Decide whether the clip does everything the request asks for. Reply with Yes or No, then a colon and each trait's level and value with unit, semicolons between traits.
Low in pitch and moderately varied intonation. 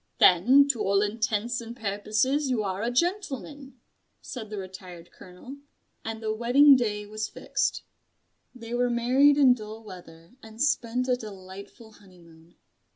No: high, 220 Hz; average, 4.0 semitones